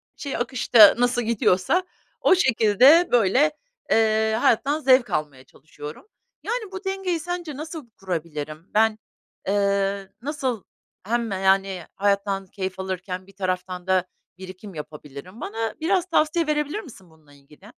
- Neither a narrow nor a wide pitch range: No, wide, 7.1 semitones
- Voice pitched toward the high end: Yes, high, 210 Hz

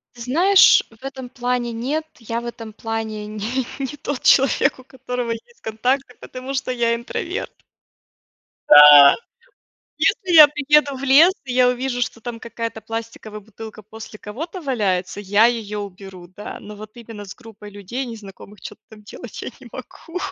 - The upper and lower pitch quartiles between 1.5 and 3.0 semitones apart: No, average, 3.6 semitones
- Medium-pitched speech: No, high, 235 Hz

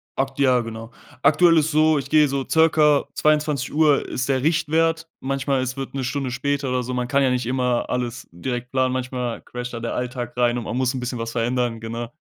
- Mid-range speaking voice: No, low, 130 Hz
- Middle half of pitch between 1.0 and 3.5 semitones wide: Yes, narrow, 2.6 semitones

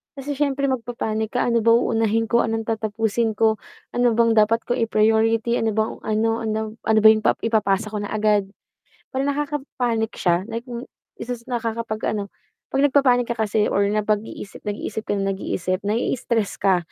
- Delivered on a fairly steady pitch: Yes, narrow, 1.8 semitones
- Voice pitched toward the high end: Yes, high, 225 Hz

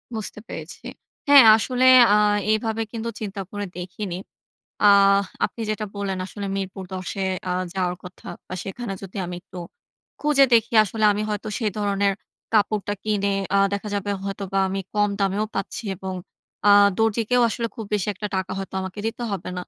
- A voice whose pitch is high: Yes, high, 205 Hz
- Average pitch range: No, narrow, 2.1 semitones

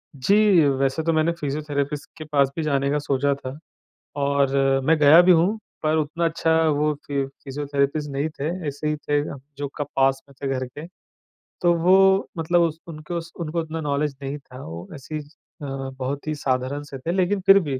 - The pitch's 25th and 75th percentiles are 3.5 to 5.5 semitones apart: No, average, 2.7 semitones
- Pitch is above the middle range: No, medium, 145 Hz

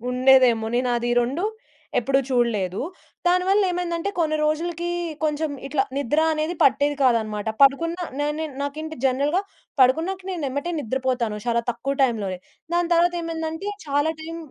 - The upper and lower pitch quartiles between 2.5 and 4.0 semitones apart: No, average, 5.0 semitones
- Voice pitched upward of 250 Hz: Yes, very high, 290 Hz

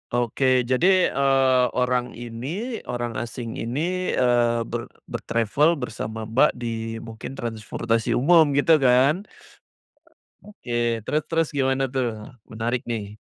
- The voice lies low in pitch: Yes, low, 125 Hz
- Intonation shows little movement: No, average, 3.2 semitones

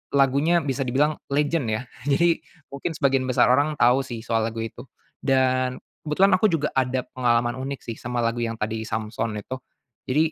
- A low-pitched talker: Yes, low, 130 Hz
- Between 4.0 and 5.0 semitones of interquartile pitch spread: No, average, 3.3 semitones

